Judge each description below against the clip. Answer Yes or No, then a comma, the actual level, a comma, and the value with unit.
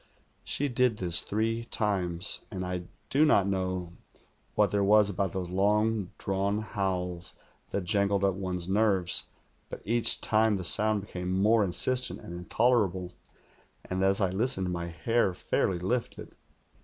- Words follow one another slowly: No, average, 145 wpm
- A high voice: No, low, 100 Hz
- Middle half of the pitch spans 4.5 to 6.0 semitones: No, average, 3.0 semitones